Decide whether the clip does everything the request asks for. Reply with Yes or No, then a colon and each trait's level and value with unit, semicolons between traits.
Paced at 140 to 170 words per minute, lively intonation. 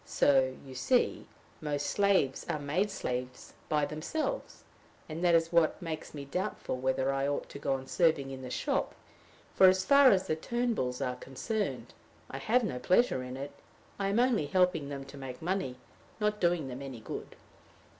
No: average, 180 wpm; wide, 6.1 semitones